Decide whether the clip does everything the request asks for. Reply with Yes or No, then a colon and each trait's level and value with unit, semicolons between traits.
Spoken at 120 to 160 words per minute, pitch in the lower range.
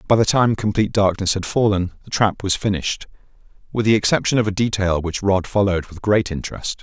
No: average, 200 wpm; low, 100 Hz